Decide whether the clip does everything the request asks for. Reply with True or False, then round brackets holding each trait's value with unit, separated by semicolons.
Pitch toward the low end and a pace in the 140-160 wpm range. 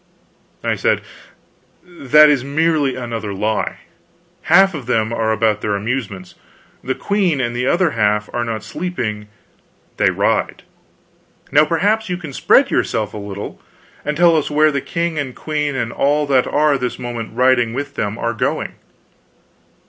True (130 Hz; 155 wpm)